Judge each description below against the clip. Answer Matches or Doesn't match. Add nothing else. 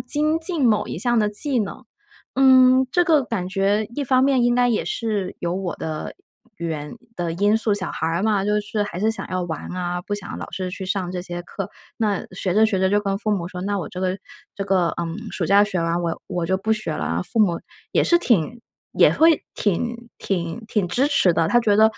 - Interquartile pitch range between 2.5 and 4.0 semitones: Doesn't match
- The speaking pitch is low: Doesn't match